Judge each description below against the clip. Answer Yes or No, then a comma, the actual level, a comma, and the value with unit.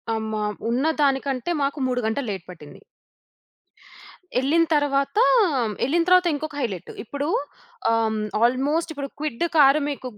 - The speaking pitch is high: Yes, very high, 275 Hz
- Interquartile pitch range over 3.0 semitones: Yes, average, 4.5 semitones